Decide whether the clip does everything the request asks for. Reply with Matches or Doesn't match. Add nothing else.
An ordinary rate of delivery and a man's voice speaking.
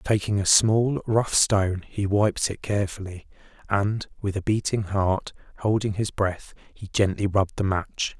Matches